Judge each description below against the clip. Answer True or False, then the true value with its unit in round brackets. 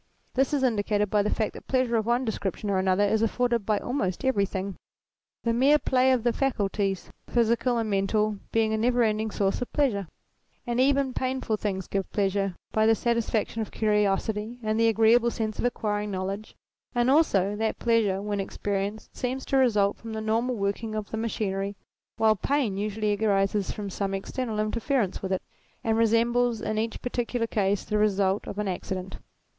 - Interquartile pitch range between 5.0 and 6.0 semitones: False (2.9 semitones)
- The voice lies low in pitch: False (215 Hz)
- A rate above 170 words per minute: True (180 wpm)